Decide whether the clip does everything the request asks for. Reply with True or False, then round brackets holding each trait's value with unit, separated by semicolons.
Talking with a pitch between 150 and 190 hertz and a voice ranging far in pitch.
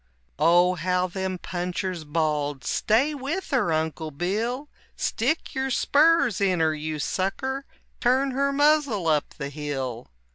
True (185 Hz; 9.0 semitones)